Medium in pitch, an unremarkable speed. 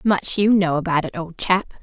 No: medium, 180 Hz; fast, 230 wpm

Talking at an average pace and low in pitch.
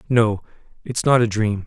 Yes: average, 180 wpm; low, 110 Hz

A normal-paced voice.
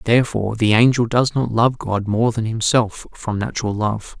Yes: average, 185 wpm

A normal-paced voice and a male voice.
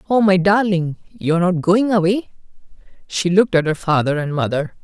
Yes: average, 175 wpm; male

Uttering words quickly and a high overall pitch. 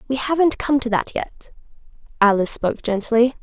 No: average, 160 wpm; high, 240 Hz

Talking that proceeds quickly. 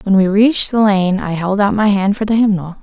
Yes: fast, 275 wpm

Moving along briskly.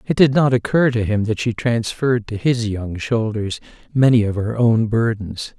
No: average, 195 wpm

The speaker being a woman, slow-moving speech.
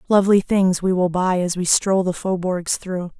No: female; fast, 205 wpm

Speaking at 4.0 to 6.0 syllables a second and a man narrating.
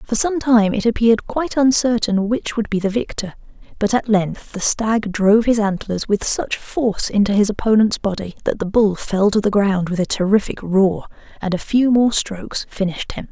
No: 5.1 syllables/s; female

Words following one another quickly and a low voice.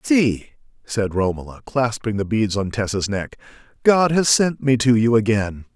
No: average, 165 wpm; low, 115 Hz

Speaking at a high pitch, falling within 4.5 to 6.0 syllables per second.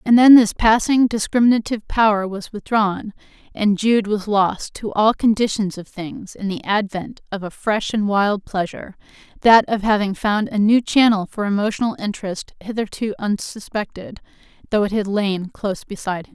Yes: high, 210 Hz; 5.0 syllables/s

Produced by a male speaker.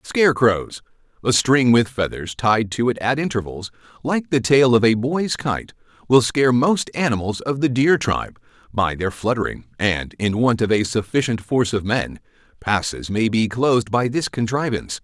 Yes: male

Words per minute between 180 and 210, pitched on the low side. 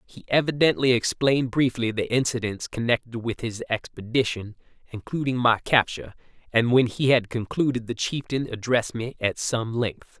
No: average, 145 wpm; low, 120 Hz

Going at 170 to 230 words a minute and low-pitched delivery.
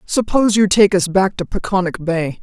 No: average, 200 wpm; high, 190 Hz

